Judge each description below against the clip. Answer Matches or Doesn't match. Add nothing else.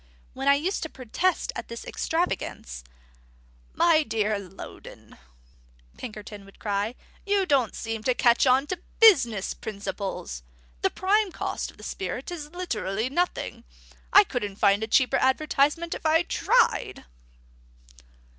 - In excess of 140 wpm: Doesn't match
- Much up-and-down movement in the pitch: Matches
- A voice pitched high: Matches